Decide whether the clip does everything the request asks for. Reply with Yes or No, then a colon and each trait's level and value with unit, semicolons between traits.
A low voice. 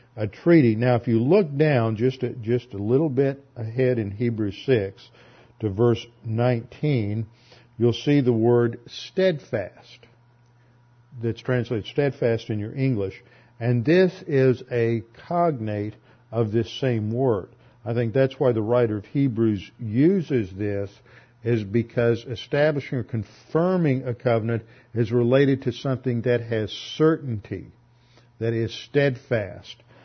Yes: low, 120 Hz